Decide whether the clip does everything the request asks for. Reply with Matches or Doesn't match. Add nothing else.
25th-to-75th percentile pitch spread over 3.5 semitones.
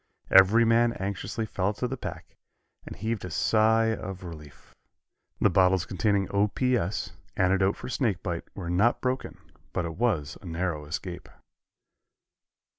Matches